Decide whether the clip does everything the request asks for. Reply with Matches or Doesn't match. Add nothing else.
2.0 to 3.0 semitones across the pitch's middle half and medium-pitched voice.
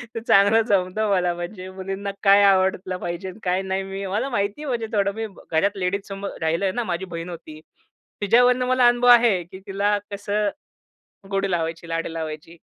Doesn't match